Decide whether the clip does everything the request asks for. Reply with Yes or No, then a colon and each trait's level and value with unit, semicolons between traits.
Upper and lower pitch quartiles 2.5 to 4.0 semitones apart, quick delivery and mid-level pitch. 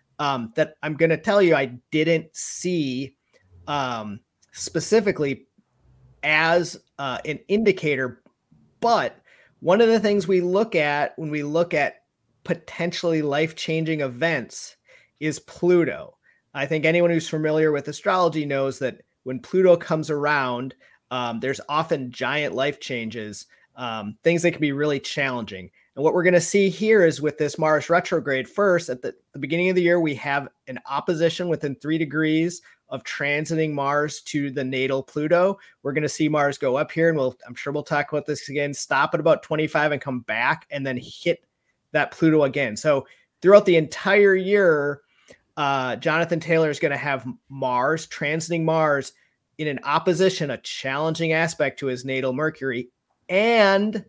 No: average, 3.6 semitones; average, 165 wpm; medium, 155 Hz